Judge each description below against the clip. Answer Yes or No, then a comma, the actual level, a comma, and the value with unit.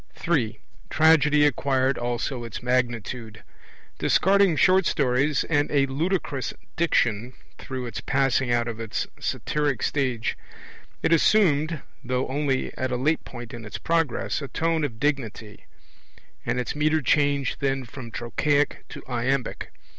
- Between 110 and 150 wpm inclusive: Yes, slow, 135 wpm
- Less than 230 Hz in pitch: Yes, low, 135 Hz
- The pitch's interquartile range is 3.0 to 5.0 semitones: Yes, average, 3.6 semitones